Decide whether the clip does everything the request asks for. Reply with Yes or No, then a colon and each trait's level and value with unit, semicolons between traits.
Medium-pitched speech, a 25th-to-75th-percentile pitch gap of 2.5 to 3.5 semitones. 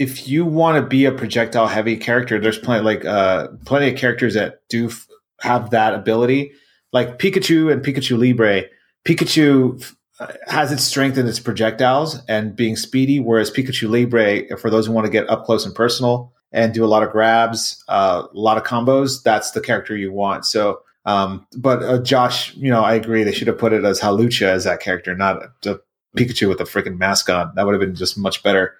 No: low, 115 Hz; average, 3.1 semitones